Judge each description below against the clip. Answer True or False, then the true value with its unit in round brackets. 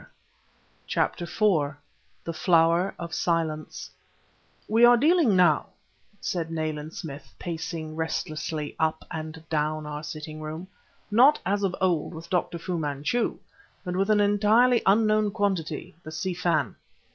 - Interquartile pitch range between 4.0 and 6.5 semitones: True (4.4 semitones)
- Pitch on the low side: False (165 Hz)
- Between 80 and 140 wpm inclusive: True (135 wpm)